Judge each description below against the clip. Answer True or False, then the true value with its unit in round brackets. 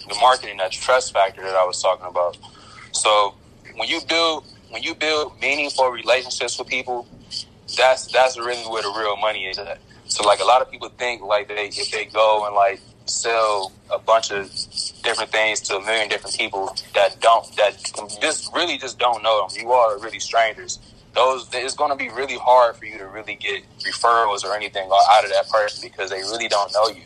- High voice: False (110 Hz)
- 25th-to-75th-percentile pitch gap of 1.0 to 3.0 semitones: False (3.7 semitones)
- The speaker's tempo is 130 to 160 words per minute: False (205 wpm)